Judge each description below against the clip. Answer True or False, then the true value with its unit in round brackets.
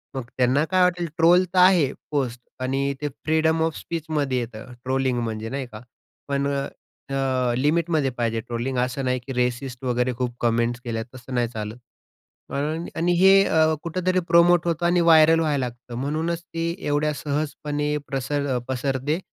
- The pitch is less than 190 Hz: True (140 Hz)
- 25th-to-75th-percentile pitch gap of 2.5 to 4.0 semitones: False (4.5 semitones)